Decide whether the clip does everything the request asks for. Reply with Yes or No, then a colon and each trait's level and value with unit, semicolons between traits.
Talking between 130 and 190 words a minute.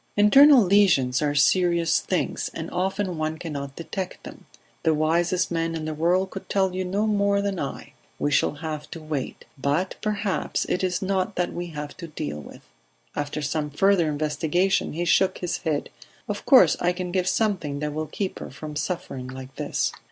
Yes: average, 185 wpm